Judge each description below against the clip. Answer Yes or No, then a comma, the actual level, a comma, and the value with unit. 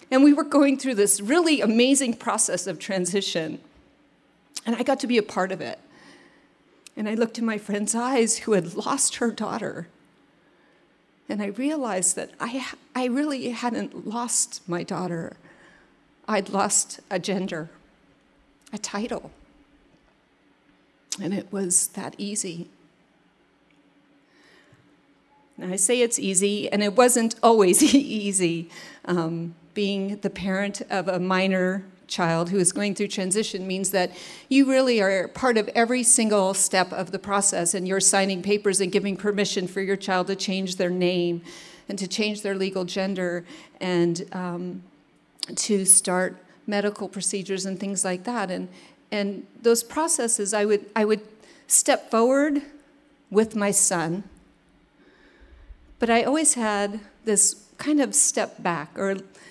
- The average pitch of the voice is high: Yes, high, 200 Hz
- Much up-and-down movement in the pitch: No, average, 3.8 semitones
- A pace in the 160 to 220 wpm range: No, average, 145 wpm